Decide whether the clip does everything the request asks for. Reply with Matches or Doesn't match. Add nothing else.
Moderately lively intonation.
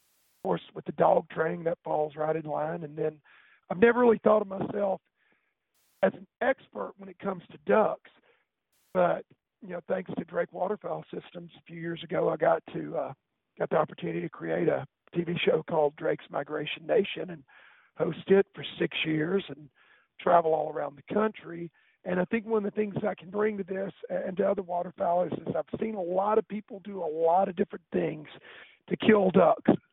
Matches